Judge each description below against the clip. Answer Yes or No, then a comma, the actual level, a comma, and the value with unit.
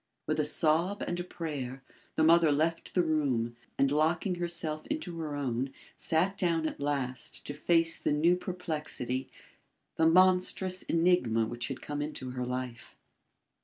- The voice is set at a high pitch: No, medium, 155 Hz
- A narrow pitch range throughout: No, average, 4.3 semitones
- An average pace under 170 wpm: Yes, average, 155 wpm